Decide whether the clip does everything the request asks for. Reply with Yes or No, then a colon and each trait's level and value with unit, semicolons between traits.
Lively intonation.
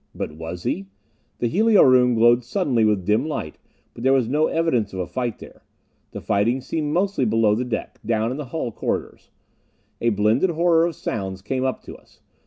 Yes: wide, 5.7 semitones